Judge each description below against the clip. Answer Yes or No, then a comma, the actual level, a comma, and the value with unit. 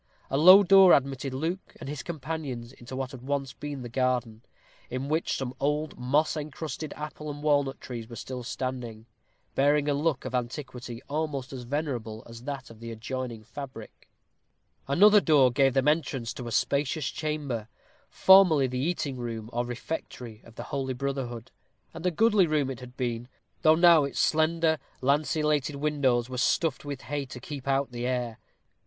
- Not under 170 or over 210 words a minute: Yes, average, 175 wpm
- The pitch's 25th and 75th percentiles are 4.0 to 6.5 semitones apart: No, average, 3.5 semitones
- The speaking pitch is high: No, low, 135 Hz